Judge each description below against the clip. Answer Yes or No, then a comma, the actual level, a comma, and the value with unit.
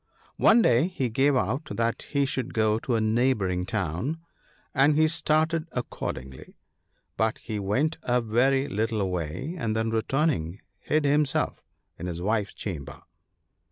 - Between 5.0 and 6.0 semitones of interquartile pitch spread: Yes, wide, 5.6 semitones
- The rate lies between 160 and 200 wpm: No, average, 145 wpm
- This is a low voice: Yes, low, 115 Hz